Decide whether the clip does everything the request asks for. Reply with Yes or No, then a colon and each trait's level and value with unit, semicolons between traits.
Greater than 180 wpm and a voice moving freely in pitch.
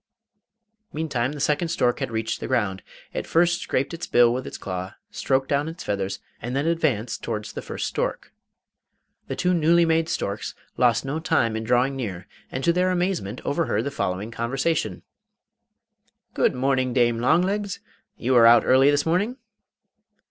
No: average, 165 wpm; wide, 5.9 semitones